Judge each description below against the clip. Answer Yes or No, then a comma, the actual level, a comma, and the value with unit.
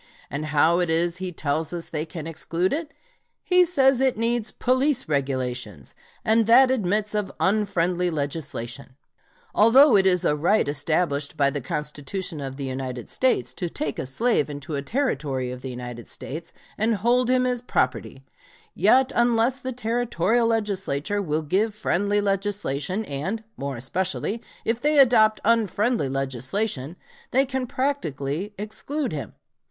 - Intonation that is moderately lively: No, wide, 8.2 semitones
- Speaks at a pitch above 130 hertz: Yes, medium, 185 Hz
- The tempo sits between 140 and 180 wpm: Yes, average, 150 wpm